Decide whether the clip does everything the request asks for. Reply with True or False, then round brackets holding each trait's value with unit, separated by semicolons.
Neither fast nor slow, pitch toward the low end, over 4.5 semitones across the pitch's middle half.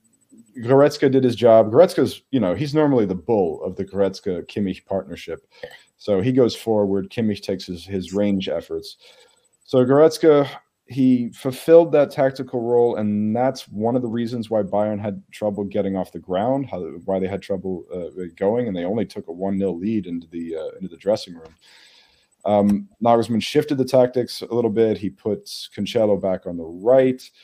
True (180 wpm; 110 Hz; 5.2 semitones)